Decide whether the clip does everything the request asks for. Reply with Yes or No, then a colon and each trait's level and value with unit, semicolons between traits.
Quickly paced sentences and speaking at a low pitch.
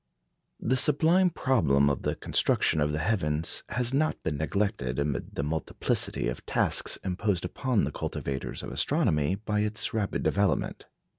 No: average, 150 wpm; very low, 95 Hz